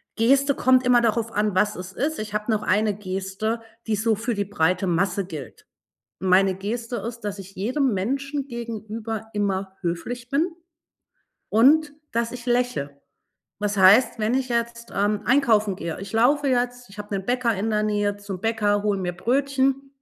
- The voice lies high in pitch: Yes, high, 220 Hz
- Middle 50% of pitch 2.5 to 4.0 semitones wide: Yes, average, 3.7 semitones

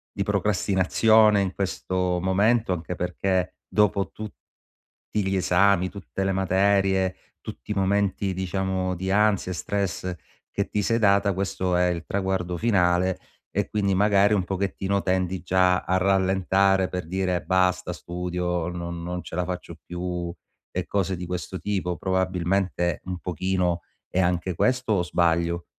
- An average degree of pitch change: No, narrow, 1.7 semitones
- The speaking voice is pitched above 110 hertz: No, very low, 95 Hz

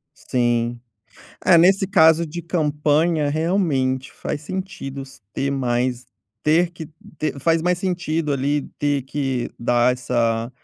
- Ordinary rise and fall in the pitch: Yes, average, 4.4 semitones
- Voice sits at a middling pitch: Yes, medium, 145 Hz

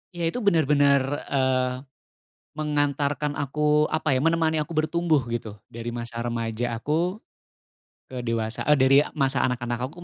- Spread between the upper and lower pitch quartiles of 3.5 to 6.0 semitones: Yes, average, 4.1 semitones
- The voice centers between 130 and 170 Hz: Yes, medium, 140 Hz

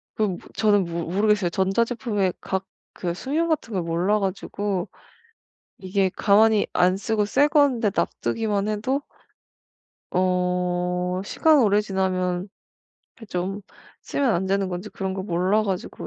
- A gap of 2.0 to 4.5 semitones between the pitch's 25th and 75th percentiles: Yes, average, 2.9 semitones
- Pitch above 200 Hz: No, high, 195 Hz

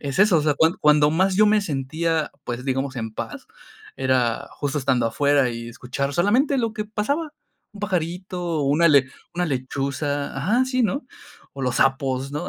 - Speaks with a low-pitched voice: No, medium, 150 Hz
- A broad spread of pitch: Yes, wide, 6.0 semitones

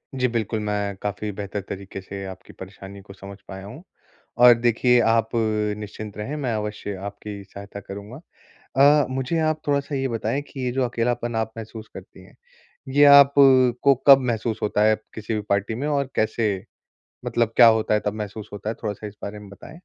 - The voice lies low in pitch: Yes, low, 110 Hz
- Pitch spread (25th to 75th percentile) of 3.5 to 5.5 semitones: Yes, average, 3.9 semitones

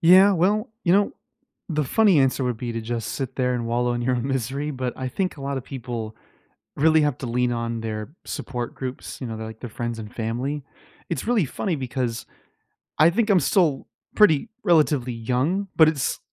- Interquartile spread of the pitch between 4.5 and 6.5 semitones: Yes, average, 5.0 semitones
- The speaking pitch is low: Yes, low, 130 Hz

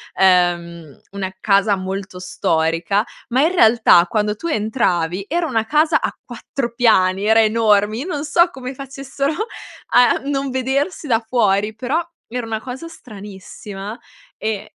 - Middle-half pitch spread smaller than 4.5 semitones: No, average, 5.2 semitones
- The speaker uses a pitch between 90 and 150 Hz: No, high, 220 Hz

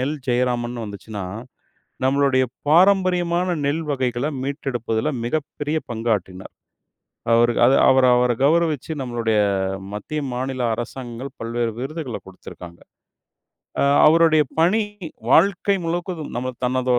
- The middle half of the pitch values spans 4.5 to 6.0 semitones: Yes, average, 4.8 semitones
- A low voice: Yes, low, 130 Hz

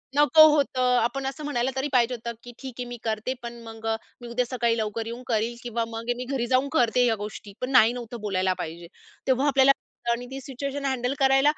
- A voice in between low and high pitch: No, high, 245 Hz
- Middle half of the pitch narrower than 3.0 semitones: Yes, narrow, 2.6 semitones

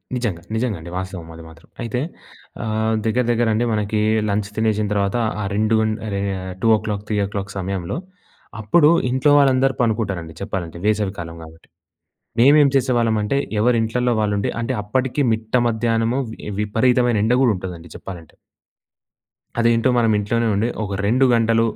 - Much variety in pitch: No, average, 3.0 semitones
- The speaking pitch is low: Yes, low, 110 Hz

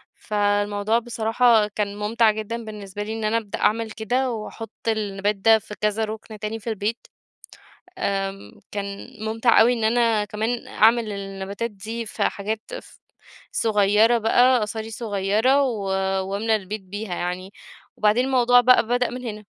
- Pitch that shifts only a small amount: Yes, narrow, 1.9 semitones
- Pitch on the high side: Yes, high, 220 Hz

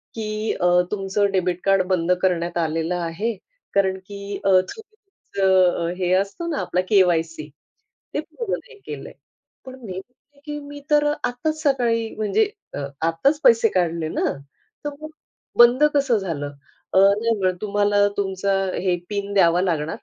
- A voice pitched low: No, high, 200 Hz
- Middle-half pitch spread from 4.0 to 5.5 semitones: Yes, average, 4.9 semitones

